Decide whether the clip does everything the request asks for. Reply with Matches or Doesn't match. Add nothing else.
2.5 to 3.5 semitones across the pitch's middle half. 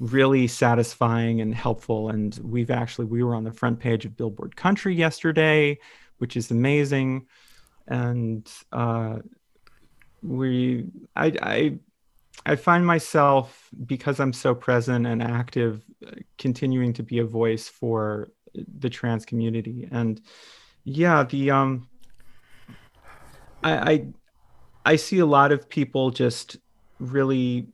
Matches